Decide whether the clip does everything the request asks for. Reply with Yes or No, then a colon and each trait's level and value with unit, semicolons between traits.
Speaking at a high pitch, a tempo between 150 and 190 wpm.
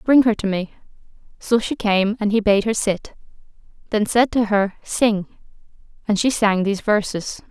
Yes: high, 210 Hz; average, 175 wpm